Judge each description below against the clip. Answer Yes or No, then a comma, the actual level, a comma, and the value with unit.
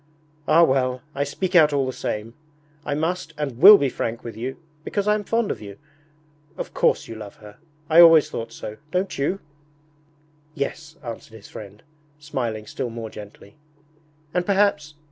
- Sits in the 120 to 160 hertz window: Yes, medium, 140 Hz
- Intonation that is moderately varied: No, wide, 6.6 semitones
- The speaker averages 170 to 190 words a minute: Yes, average, 175 wpm